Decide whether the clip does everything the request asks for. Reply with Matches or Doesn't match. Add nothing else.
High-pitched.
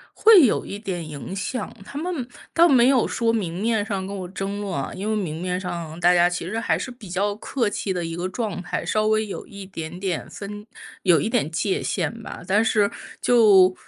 Matches